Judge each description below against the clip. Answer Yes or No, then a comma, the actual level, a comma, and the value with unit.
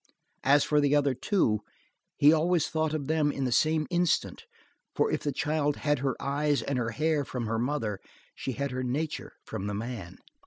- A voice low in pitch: No, medium, 145 Hz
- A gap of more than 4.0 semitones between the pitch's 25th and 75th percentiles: No, average, 3.5 semitones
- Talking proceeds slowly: No, average, 195 wpm